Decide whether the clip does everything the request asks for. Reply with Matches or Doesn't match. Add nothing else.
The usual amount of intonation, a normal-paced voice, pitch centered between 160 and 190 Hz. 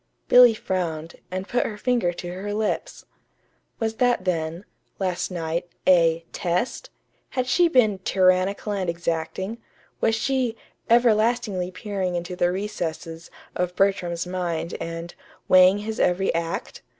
Doesn't match